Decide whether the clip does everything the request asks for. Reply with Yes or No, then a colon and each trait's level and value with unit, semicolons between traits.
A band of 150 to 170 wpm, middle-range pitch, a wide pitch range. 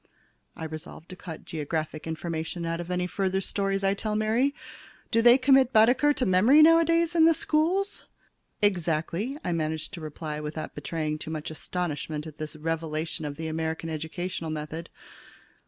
Yes: average, 160 wpm; medium, 170 Hz; wide, 5.9 semitones